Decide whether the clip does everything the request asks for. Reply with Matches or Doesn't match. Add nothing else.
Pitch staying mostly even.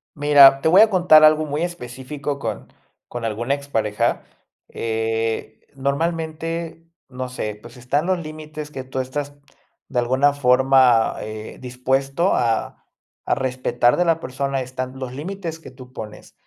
Doesn't match